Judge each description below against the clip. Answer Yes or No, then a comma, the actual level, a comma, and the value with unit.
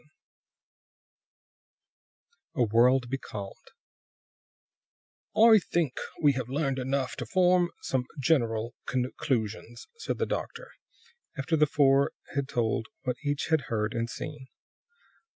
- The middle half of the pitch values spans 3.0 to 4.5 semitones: Yes, average, 3.9 semitones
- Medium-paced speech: No, slow, 115 wpm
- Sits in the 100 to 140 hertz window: Yes, low, 135 Hz